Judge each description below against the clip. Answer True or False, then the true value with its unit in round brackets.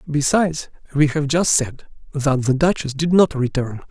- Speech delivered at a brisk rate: False (170 wpm)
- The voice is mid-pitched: True (145 Hz)